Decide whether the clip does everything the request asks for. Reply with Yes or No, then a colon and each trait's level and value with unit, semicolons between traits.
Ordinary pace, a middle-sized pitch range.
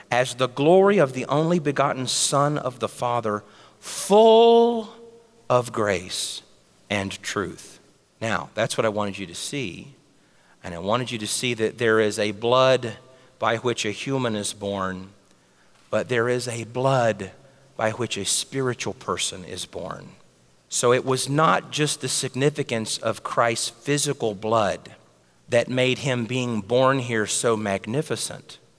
Yes: average, 150 wpm; average, 3.8 semitones